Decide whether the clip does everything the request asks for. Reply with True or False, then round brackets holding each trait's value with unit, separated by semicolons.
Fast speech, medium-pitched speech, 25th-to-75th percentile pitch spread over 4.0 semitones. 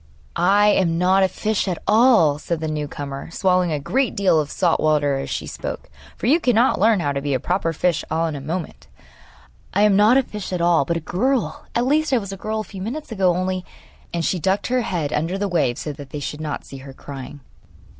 True (245 wpm; 180 Hz; 5.6 semitones)